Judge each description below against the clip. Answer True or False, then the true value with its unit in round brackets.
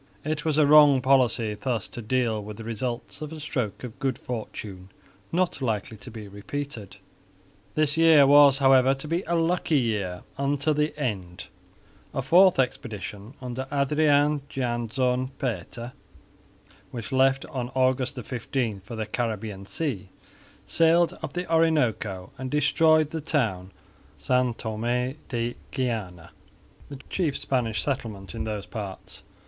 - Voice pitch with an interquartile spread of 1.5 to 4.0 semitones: False (4.8 semitones)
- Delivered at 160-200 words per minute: False (145 wpm)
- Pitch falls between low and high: False (125 Hz)